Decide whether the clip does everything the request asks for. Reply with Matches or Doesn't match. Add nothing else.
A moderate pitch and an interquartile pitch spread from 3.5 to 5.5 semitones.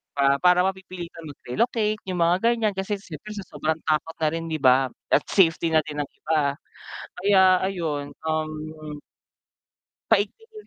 Matches